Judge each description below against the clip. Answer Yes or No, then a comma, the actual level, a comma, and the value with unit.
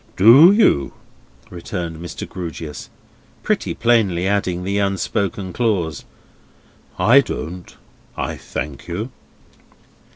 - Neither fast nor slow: No, slow, 95 wpm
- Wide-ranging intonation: No, average, 4.1 semitones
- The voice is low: Yes, very low, 95 Hz